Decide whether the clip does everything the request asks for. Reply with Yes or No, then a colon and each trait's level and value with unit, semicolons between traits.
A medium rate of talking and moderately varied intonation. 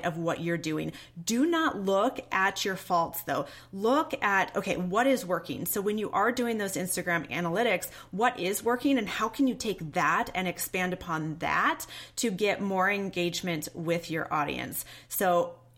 Yes: average, 175 wpm; average, 3.8 semitones